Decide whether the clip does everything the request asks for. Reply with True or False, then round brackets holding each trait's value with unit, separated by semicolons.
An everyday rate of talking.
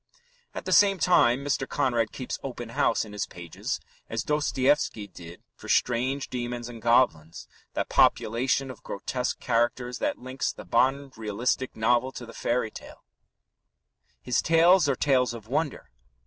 True (150 wpm)